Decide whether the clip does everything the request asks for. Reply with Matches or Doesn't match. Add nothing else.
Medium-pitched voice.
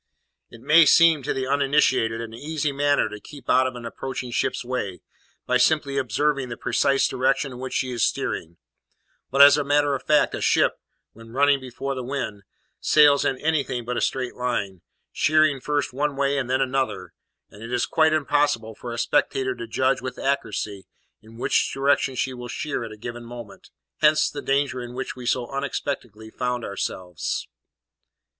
Doesn't match